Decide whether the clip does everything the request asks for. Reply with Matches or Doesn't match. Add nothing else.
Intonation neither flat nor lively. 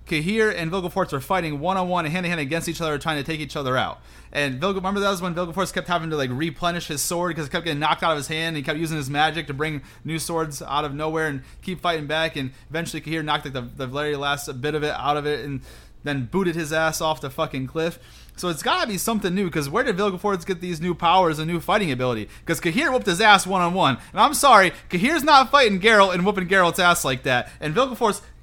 Matches